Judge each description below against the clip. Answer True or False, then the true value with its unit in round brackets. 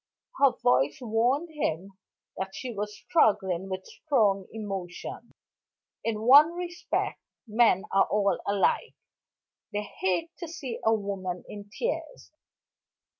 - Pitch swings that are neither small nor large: False (5.7 semitones)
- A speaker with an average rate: False (120 wpm)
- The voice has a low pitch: False (210 Hz)